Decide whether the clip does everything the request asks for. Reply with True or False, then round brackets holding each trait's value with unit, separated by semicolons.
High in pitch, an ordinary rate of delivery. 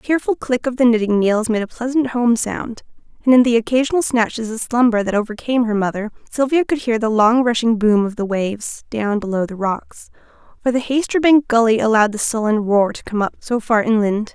False (230 Hz; 215 wpm)